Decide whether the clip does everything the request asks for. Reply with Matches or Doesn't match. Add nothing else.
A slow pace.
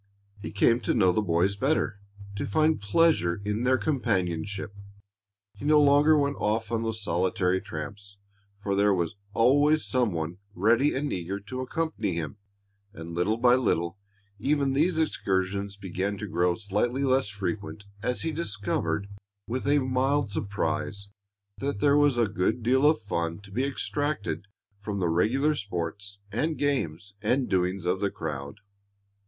Doesn't match